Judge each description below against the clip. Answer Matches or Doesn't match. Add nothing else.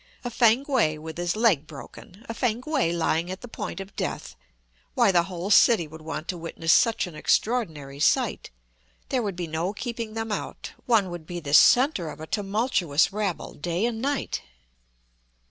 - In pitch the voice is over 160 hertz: Matches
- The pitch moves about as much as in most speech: Doesn't match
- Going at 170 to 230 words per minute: Matches